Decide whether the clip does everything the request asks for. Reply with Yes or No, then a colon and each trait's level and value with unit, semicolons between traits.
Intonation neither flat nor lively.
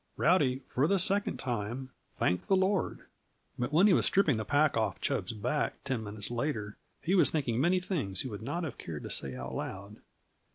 No: wide, 8.0 semitones